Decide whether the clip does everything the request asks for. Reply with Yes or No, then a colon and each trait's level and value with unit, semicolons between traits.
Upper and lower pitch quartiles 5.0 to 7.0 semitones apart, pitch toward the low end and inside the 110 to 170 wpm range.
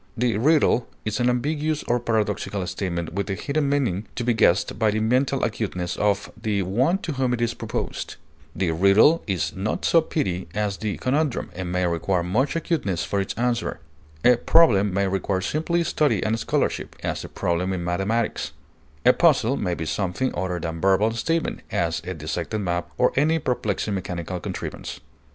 No: wide, 5.4 semitones; low, 110 Hz; average, 180 wpm